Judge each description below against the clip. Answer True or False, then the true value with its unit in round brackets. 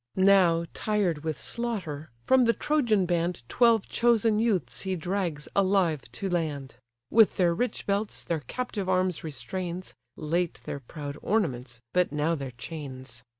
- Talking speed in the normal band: True (145 wpm)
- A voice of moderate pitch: True (175 Hz)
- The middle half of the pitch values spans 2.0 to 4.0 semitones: False (5.3 semitones)